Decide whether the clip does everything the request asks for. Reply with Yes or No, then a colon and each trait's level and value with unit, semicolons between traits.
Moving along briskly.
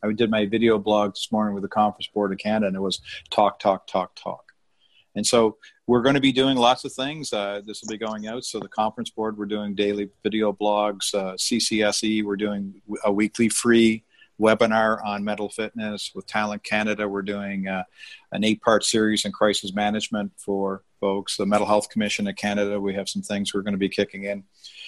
Yes: fast, 210 wpm